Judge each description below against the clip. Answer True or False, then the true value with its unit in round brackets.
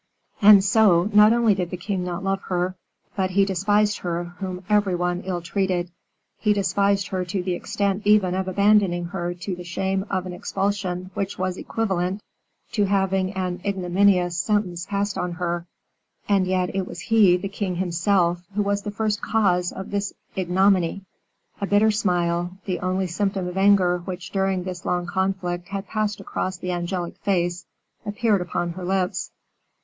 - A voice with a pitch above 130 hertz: True (190 Hz)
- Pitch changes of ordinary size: False (2.1 semitones)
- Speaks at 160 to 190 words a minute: True (170 wpm)